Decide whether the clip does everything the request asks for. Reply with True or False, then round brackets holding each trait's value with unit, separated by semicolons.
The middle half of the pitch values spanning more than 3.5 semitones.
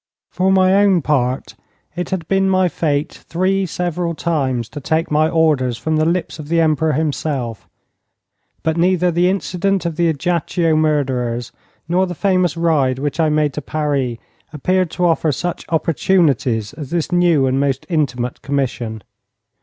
True (4.0 semitones)